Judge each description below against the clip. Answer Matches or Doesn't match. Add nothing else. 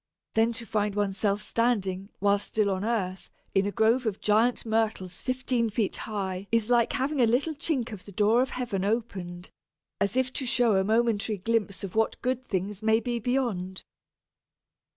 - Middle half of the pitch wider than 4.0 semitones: Doesn't match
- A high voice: Matches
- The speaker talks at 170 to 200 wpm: Matches